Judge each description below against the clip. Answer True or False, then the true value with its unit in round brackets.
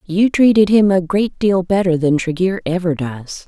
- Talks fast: False (190 wpm)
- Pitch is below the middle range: False (185 Hz)